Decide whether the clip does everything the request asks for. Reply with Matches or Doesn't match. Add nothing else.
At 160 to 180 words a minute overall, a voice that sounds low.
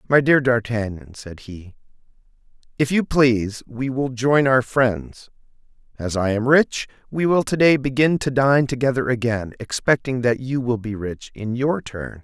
Matches